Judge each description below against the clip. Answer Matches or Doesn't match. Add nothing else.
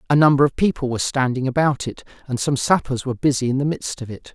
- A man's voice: Matches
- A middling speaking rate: Doesn't match